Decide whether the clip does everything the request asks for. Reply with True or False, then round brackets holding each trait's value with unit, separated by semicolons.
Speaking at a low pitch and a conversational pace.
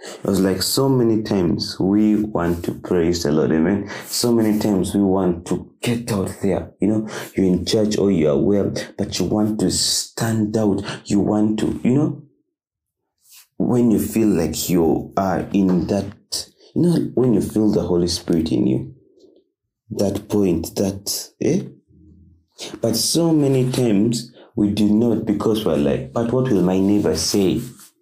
True (105 Hz; 175 wpm)